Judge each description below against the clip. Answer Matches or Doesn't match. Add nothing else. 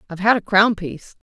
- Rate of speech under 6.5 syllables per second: Doesn't match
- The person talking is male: Doesn't match